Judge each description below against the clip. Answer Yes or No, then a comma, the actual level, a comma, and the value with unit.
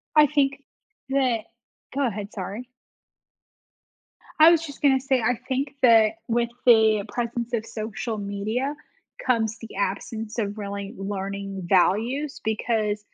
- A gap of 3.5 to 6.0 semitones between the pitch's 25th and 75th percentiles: Yes, average, 4.0 semitones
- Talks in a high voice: Yes, high, 225 Hz